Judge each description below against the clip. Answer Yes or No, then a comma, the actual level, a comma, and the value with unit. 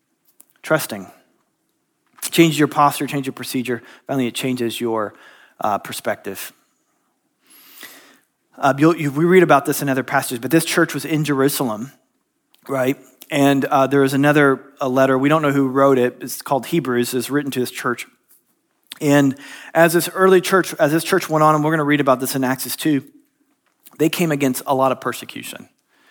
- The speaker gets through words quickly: No, average, 180 wpm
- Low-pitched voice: No, medium, 145 Hz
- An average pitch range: Yes, average, 3.8 semitones